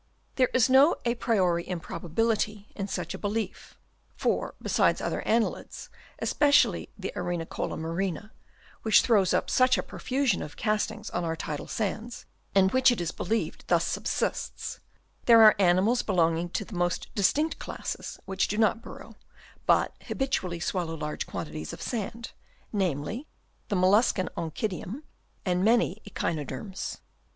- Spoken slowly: No, average, 145 wpm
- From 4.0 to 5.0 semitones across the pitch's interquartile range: Yes, average, 4.7 semitones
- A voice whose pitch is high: Yes, high, 200 Hz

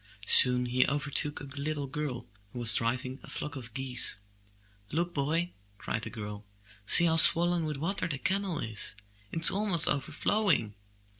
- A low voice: No, medium, 145 Hz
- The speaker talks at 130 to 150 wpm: No, average, 160 wpm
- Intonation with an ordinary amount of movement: Yes, average, 4.9 semitones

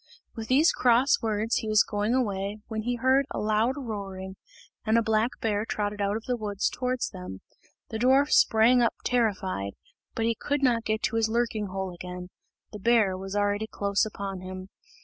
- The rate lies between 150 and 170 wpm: No, average, 190 wpm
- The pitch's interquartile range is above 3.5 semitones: No, average, 2.8 semitones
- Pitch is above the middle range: Yes, high, 215 Hz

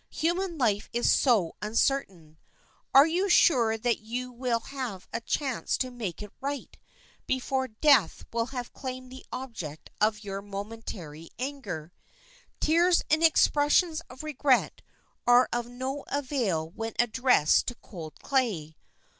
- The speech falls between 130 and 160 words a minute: Yes, slow, 135 wpm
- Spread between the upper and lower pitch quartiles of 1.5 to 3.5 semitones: No, average, 4.7 semitones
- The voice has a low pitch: No, high, 245 Hz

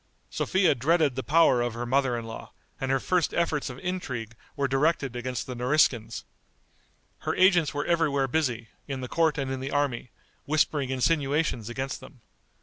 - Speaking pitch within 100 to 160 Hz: Yes, low, 135 Hz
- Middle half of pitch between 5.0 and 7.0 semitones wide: No, average, 3.7 semitones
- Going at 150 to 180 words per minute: Yes, average, 170 wpm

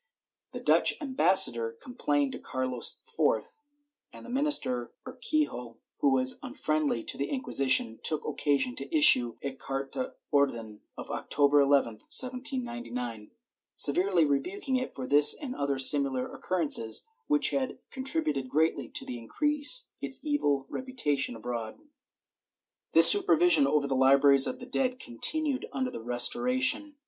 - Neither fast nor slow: No, slow, 130 wpm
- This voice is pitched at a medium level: Yes, medium, 150 Hz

